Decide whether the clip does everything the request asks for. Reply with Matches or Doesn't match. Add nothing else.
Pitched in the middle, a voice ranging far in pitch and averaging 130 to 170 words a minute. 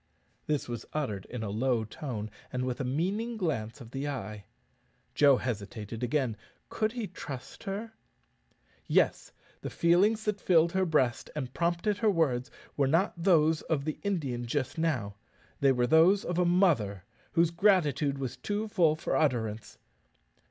Matches